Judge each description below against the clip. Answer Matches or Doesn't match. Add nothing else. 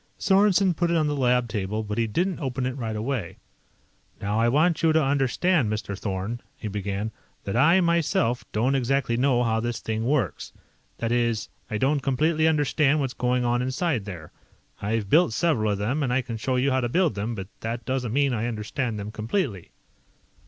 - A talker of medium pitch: Doesn't match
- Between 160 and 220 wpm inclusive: Matches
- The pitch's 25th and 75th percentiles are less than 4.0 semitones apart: Doesn't match